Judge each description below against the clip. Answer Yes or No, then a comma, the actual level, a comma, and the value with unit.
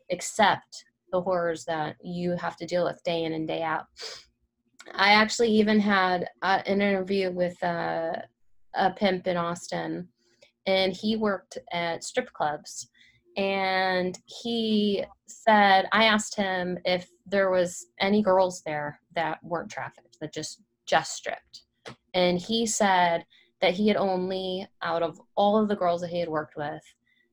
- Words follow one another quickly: No, average, 155 wpm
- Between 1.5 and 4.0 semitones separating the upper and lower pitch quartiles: Yes, average, 2.8 semitones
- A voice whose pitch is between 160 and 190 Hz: Yes, medium, 185 Hz